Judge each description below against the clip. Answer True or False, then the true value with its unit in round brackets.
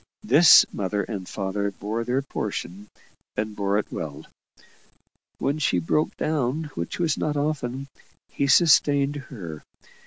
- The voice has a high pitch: False (125 Hz)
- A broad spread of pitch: True (6.3 semitones)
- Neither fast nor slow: False (130 wpm)